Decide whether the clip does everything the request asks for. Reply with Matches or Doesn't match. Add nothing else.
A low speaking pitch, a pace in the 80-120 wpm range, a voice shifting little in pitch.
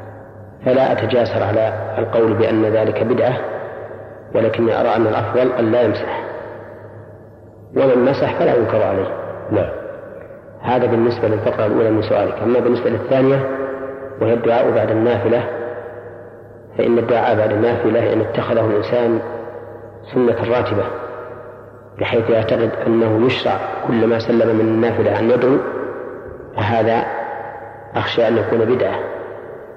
Matches